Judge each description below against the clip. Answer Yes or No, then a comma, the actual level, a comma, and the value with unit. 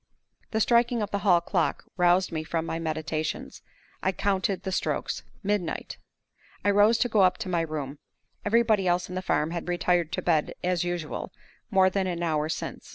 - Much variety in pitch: No, average, 3.4 semitones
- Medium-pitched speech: Yes, medium, 180 Hz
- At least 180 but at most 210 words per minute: Yes, average, 185 wpm